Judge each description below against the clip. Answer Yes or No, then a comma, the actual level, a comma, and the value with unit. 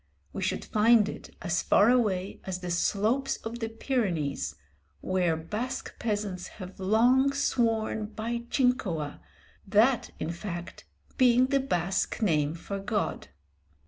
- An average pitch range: Yes, average, 4.7 semitones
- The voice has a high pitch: Yes, high, 210 Hz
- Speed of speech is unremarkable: No, slow, 130 wpm